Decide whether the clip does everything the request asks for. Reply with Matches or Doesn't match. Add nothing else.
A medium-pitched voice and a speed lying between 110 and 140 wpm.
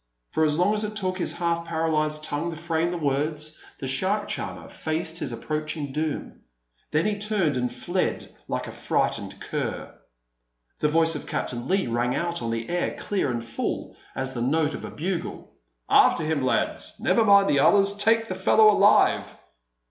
Doesn't match